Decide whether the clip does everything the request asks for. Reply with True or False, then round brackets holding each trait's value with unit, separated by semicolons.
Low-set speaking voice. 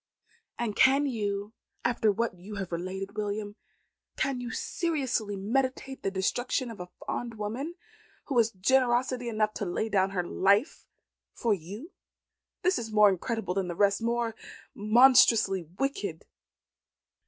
False (215 Hz)